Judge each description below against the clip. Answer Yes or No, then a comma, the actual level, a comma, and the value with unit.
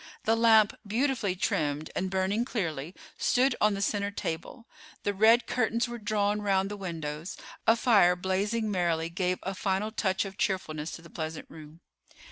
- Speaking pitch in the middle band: No, high, 195 Hz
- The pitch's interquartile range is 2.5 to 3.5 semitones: No, average, 4.0 semitones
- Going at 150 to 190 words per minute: Yes, average, 165 wpm